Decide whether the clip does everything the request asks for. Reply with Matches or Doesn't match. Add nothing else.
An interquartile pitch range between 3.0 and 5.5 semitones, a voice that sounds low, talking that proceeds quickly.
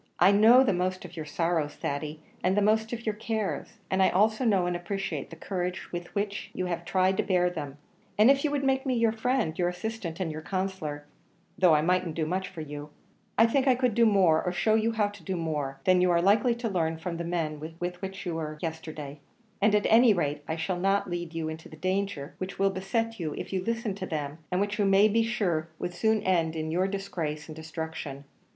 Doesn't match